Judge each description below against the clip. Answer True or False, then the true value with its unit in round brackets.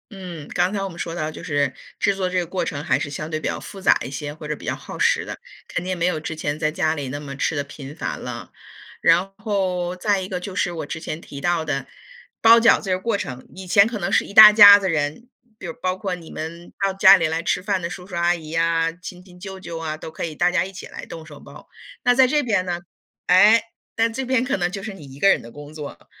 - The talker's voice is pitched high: False (175 Hz)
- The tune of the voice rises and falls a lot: False (3.8 semitones)